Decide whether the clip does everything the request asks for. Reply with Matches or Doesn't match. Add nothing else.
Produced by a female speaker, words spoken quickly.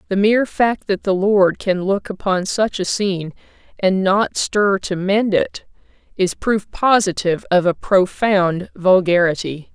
Doesn't match